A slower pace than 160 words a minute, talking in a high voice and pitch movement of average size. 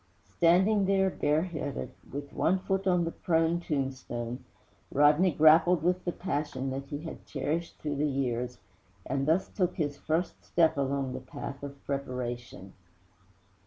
No: average, 145 wpm; medium, 150 Hz; average, 4.2 semitones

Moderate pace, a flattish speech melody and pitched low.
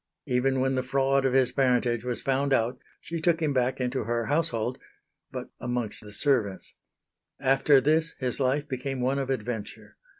Yes: average, 170 wpm; narrow, 2.0 semitones; low, 130 Hz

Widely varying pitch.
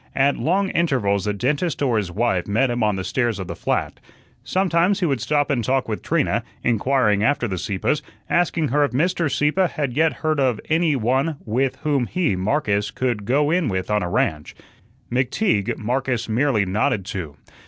Yes: wide, 6.1 semitones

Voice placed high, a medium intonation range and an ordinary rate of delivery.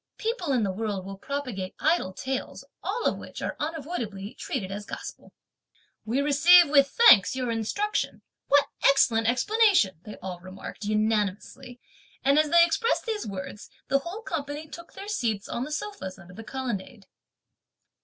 No: very high, 260 Hz; wide, 7.7 semitones; average, 155 wpm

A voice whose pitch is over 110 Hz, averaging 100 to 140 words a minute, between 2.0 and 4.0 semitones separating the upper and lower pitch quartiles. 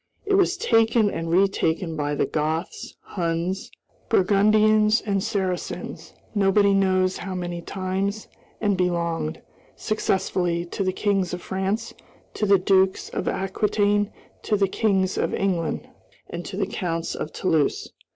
Yes: high, 190 Hz; slow, 135 wpm; average, 2.7 semitones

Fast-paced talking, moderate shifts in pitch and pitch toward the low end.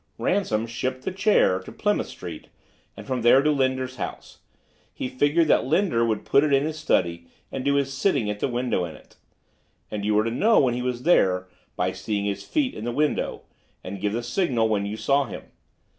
Yes: fast, 215 wpm; average, 4.9 semitones; low, 125 Hz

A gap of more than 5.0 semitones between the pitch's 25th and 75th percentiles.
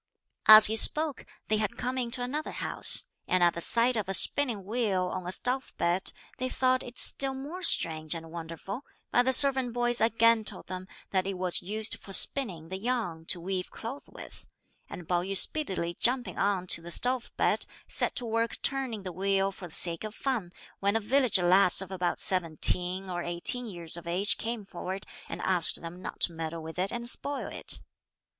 Yes: wide, 5.4 semitones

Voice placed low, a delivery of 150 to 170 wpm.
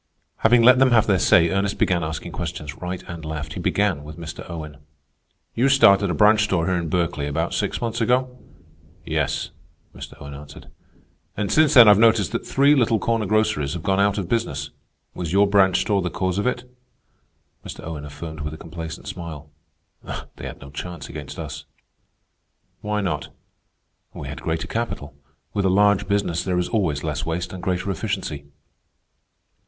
No: very low, 90 Hz; average, 180 wpm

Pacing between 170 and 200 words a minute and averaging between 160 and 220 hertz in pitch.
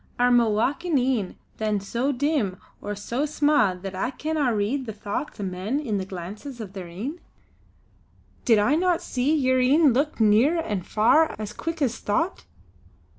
No: average, 175 wpm; high, 245 Hz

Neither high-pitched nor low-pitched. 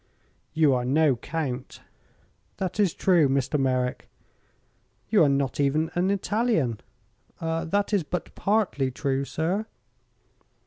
Yes: medium, 160 Hz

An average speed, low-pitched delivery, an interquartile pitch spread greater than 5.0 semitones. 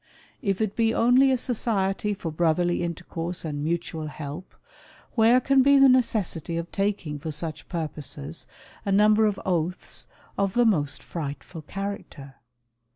No: average, 145 wpm; medium, 180 Hz; wide, 5.4 semitones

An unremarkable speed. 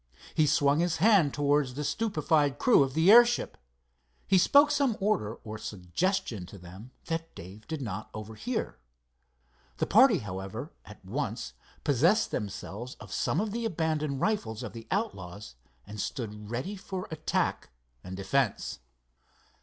Yes: average, 145 wpm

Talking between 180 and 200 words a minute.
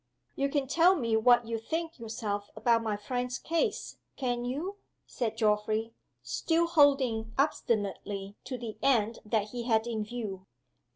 No: average, 150 wpm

